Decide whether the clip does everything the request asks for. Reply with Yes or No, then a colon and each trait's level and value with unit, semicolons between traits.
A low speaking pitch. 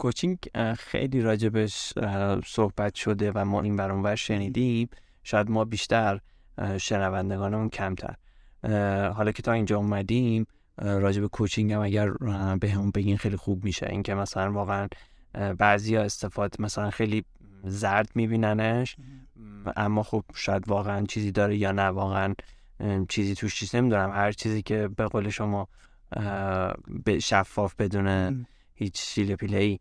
Yes: low, 105 Hz